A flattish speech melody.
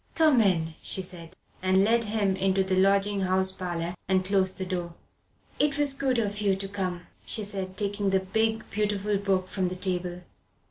Yes: narrow, 1.8 semitones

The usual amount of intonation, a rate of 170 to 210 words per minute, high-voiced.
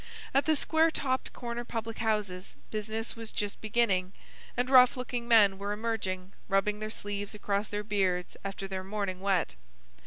No: average, 3.0 semitones; average, 160 wpm; high, 210 Hz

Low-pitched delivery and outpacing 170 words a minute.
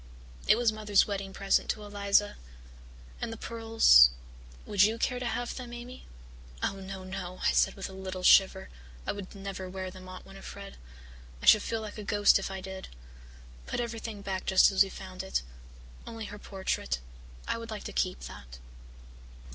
No: high, 200 Hz; average, 180 wpm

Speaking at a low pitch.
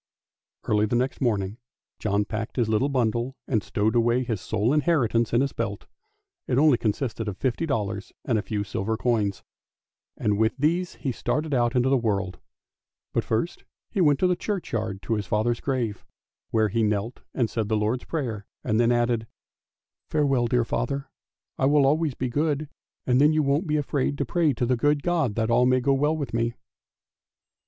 Yes: low, 120 Hz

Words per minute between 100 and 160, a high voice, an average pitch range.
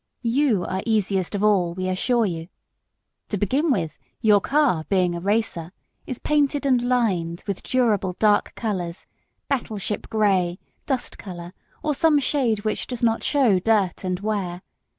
Yes: average, 150 wpm; high, 210 Hz; average, 5.0 semitones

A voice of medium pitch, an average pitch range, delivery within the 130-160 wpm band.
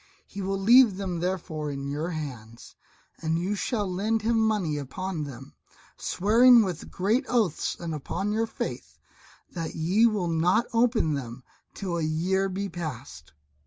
Yes: medium, 180 Hz; average, 5.0 semitones; average, 155 wpm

